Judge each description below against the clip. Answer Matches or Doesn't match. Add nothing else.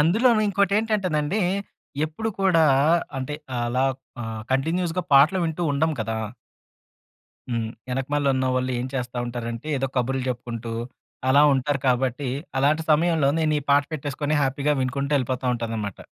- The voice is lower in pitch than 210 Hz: Matches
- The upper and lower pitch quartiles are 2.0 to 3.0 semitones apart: Doesn't match